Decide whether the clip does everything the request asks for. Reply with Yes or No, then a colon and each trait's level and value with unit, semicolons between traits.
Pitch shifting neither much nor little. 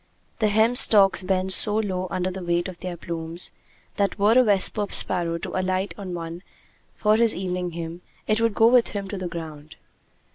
Yes: average, 3.3 semitones